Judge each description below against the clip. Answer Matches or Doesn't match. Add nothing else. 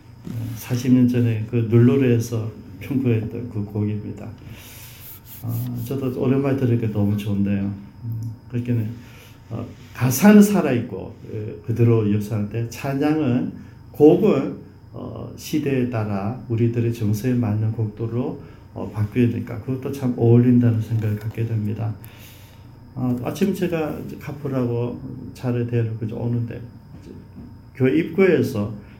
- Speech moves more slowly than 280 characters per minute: Matches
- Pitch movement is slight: Matches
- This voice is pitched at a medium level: Doesn't match